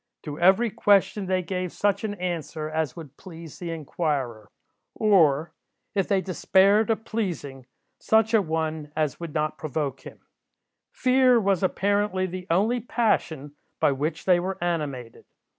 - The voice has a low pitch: No, medium, 175 Hz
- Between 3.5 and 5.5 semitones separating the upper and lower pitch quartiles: Yes, average, 4.7 semitones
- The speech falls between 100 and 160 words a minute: Yes, average, 145 wpm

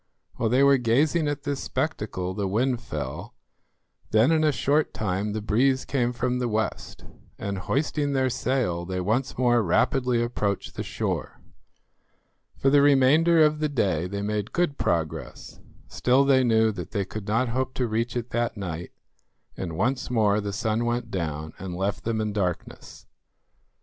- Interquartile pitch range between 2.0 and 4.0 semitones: No, average, 4.7 semitones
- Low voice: Yes, low, 120 Hz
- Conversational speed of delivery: Yes, average, 170 wpm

